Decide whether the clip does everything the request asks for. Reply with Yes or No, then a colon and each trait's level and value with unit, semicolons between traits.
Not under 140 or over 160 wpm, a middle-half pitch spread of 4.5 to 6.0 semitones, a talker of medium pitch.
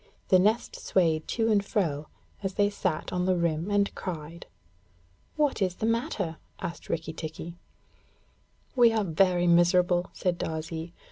No: average, 145 wpm; average, 3.5 semitones; medium, 180 Hz